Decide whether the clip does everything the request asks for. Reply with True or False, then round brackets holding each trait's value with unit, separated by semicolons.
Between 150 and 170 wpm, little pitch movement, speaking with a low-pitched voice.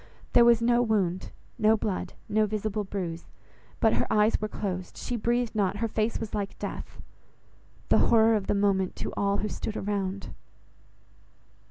False (165 wpm; 2.0 semitones; 210 Hz)